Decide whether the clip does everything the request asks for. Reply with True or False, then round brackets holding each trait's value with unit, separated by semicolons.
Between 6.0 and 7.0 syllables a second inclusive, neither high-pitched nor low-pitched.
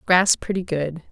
False (4.3 syllables/s; 170 Hz)